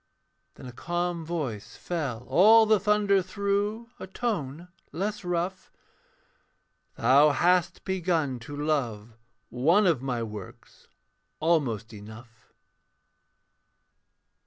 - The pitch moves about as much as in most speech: No, wide, 7.4 semitones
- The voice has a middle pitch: Yes, medium, 165 Hz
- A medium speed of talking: No, slow, 100 wpm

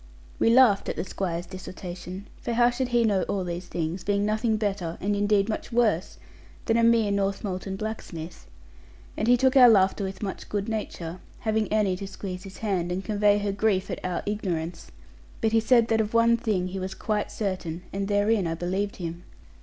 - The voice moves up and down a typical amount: Yes, average, 3.0 semitones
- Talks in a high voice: Yes, high, 200 Hz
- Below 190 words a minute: No, average, 195 wpm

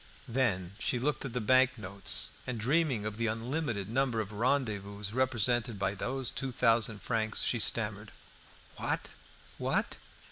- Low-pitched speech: Yes, low, 115 Hz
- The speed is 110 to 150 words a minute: Yes, average, 145 wpm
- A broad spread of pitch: No, average, 3.6 semitones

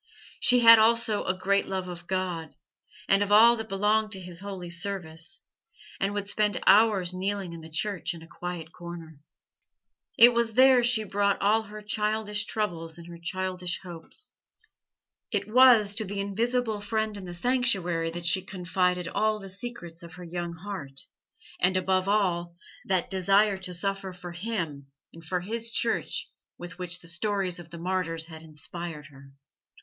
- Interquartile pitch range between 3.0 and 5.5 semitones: Yes, average, 3.5 semitones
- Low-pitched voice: No, high, 190 Hz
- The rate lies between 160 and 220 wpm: Yes, average, 170 wpm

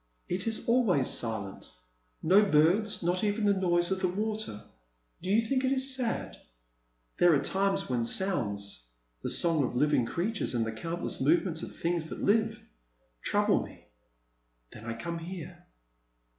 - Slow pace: No, average, 165 wpm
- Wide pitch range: Yes, wide, 7.9 semitones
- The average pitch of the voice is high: No, medium, 175 Hz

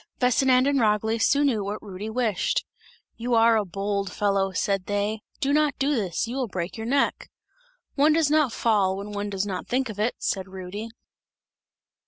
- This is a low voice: No, high, 215 Hz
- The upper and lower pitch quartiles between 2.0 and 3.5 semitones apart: No, average, 4.2 semitones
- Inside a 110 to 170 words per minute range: No, average, 185 wpm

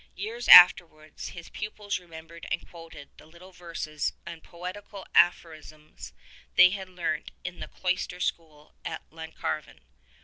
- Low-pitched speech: No, medium, 170 Hz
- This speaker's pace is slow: Yes, slow, 130 wpm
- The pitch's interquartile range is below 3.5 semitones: Yes, narrow, 2.4 semitones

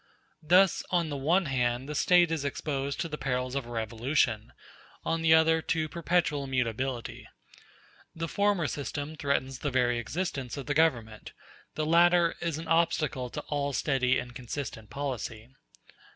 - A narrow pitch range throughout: No, average, 4.4 semitones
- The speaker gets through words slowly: No, average, 155 wpm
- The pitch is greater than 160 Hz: No, medium, 145 Hz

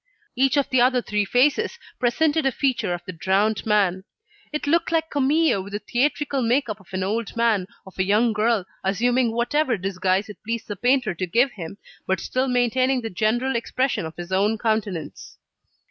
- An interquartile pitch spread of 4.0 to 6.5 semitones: Yes, average, 4.8 semitones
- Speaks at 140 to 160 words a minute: No, average, 190 wpm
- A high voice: Yes, high, 230 Hz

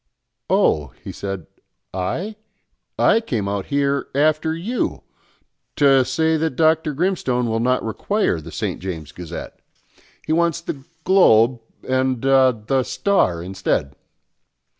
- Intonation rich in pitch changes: Yes, wide, 7.9 semitones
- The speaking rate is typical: No, slow, 125 wpm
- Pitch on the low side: Yes, low, 130 Hz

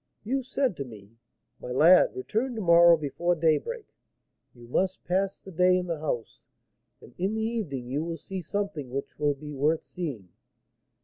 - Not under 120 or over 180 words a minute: Yes, average, 175 wpm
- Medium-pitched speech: Yes, medium, 170 Hz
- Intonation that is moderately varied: No, wide, 5.9 semitones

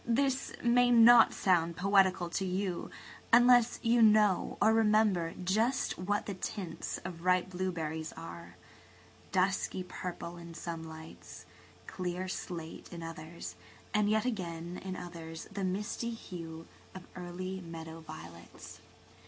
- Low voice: No, medium, 185 Hz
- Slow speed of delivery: Yes, slow, 125 wpm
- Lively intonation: No, average, 3.9 semitones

